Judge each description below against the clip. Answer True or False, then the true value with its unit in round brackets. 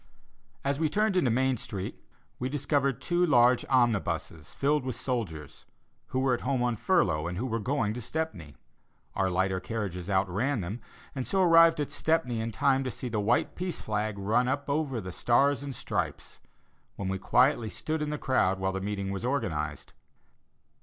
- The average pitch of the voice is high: False (120 Hz)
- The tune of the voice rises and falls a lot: True (6.3 semitones)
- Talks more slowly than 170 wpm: False (180 wpm)